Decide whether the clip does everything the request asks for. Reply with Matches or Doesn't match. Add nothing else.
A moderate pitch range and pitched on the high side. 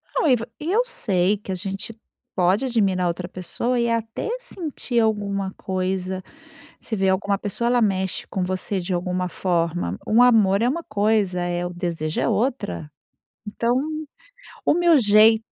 Matches